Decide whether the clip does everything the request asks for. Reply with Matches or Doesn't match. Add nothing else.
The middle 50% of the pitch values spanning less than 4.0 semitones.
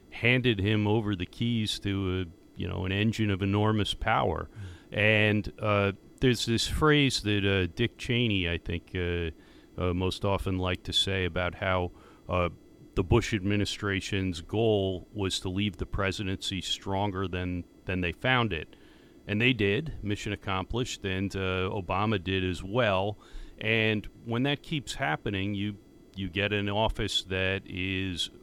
Matches